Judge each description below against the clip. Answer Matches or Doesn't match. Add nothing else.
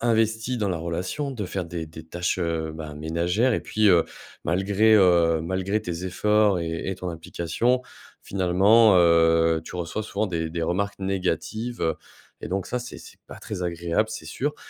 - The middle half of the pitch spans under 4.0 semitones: Doesn't match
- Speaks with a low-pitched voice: Matches